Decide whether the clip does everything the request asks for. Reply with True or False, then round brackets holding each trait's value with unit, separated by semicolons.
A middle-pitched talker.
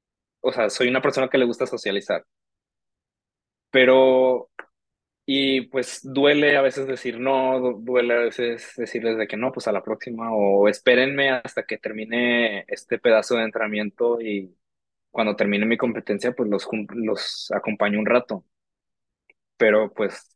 False (120 Hz)